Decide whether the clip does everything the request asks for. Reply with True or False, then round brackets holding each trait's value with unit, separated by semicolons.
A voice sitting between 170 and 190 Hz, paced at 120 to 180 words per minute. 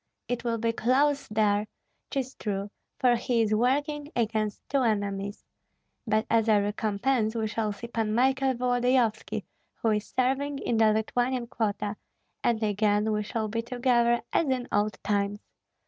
False (225 Hz; 155 wpm)